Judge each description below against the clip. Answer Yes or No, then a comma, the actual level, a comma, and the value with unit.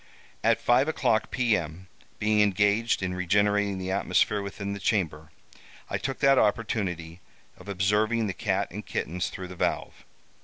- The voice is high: No, low, 100 Hz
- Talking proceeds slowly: No, average, 150 wpm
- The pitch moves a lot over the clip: No, average, 2.7 semitones